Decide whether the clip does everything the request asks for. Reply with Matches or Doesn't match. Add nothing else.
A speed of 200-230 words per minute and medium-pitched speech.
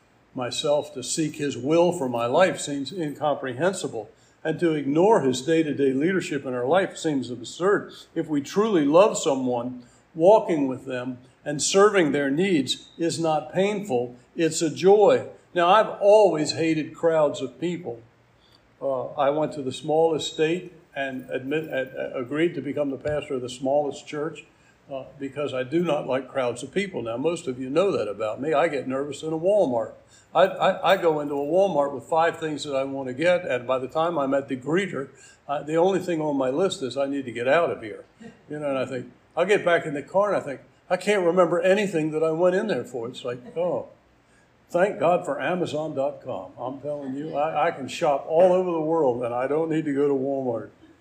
Matches